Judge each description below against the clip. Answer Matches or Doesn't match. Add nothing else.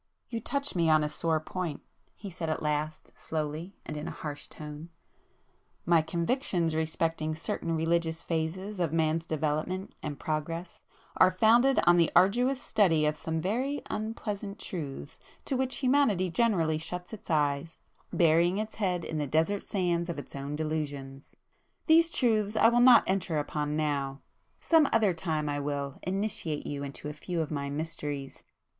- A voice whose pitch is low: Doesn't match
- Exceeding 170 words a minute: Doesn't match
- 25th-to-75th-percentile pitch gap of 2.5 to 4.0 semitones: Doesn't match